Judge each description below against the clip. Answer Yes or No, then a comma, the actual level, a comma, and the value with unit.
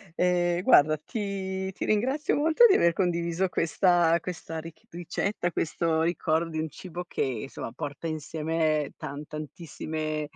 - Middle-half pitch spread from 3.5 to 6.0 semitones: No, narrow, 2.6 semitones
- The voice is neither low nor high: Yes, medium, 165 Hz